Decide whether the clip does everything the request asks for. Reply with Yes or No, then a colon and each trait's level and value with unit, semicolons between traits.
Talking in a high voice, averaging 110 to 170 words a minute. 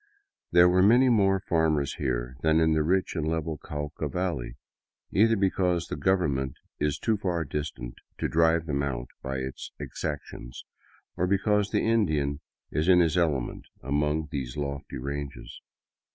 No: very low, 80 Hz; average, 155 wpm